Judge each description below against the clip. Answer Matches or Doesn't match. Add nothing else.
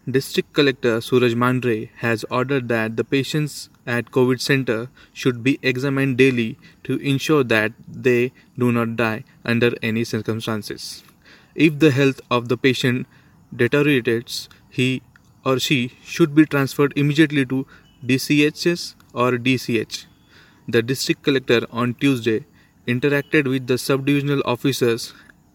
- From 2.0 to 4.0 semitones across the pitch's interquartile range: Matches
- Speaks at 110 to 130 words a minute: Matches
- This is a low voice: Matches